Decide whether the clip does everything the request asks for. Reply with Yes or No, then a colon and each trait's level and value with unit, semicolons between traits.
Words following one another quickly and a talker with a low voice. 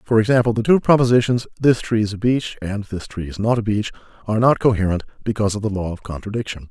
Yes: fast, 235 wpm; low, 110 Hz